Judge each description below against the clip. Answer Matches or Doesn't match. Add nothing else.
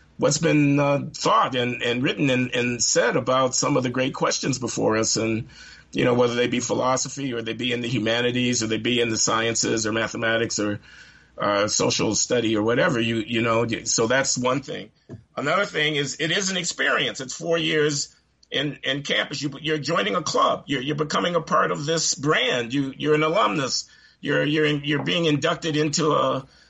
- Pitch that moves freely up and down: Doesn't match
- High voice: Doesn't match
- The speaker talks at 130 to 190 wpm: Doesn't match